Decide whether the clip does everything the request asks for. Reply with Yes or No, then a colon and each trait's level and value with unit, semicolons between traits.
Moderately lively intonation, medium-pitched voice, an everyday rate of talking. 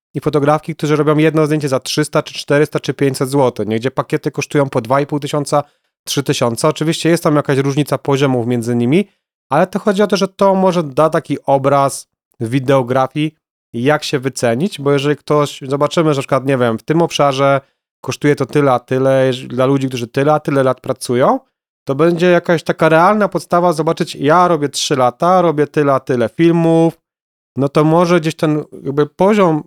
No: average, 3.1 semitones; medium, 150 Hz; fast, 180 wpm